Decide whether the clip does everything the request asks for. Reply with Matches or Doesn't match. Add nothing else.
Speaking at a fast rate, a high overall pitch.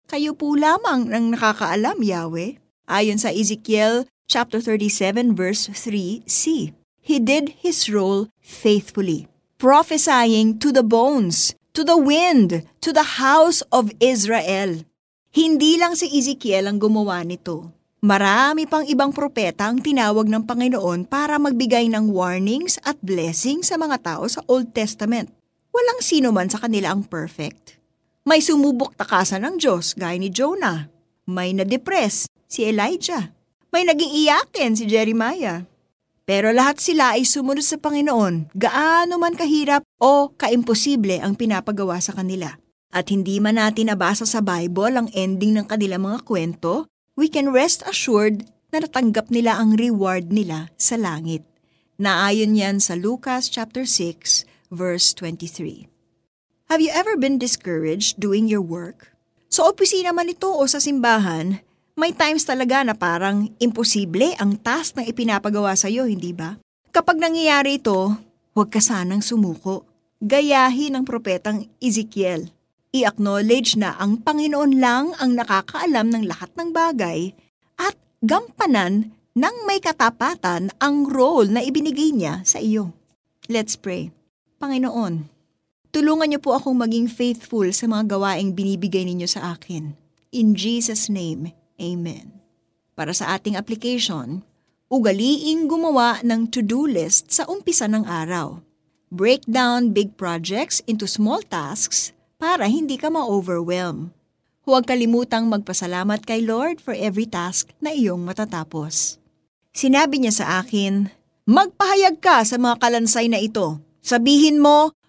Doesn't match